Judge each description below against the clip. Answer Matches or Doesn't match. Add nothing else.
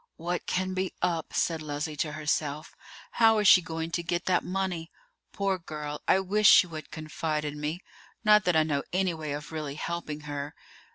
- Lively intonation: Doesn't match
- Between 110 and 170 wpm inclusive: Doesn't match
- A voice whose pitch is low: Doesn't match